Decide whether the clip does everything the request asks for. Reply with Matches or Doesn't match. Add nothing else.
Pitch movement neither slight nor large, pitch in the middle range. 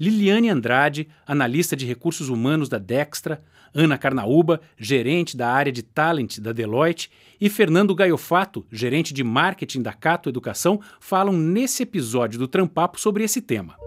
Doesn't match